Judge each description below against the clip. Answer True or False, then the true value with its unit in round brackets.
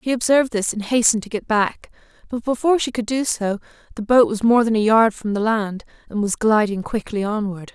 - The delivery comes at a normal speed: False (225 wpm)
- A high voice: True (220 Hz)